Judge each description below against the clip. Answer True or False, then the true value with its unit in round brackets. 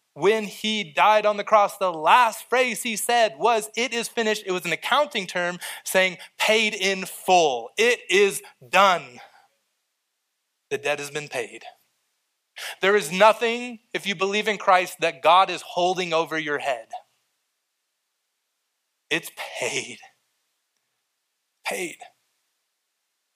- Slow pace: True (130 wpm)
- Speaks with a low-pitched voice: False (210 Hz)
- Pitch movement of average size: True (4.2 semitones)